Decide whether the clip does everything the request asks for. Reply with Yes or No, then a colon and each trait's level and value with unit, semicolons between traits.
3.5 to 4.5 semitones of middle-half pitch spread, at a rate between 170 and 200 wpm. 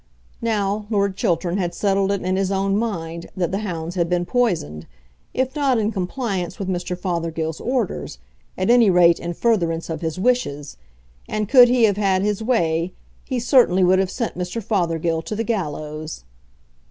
Yes: average, 4.2 semitones; average, 175 wpm